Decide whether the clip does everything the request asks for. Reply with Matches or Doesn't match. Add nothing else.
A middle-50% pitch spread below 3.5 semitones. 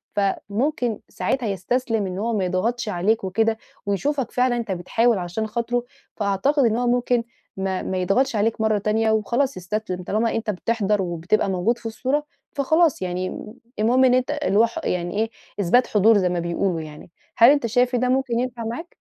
Doesn't match